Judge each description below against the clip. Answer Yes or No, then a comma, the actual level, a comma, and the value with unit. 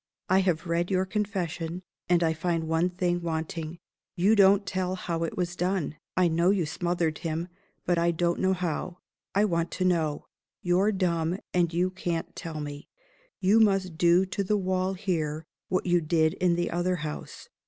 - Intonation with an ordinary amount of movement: No, narrow, 2.1 semitones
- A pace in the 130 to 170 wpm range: No, average, 180 wpm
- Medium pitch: Yes, medium, 175 Hz